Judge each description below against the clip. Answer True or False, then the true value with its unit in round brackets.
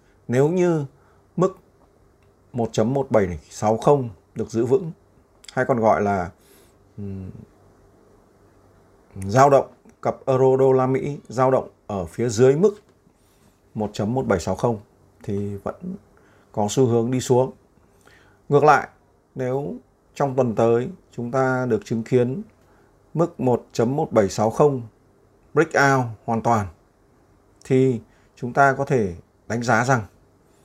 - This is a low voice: True (115 Hz)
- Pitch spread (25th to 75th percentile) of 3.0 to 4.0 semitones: False (4.7 semitones)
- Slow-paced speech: True (115 wpm)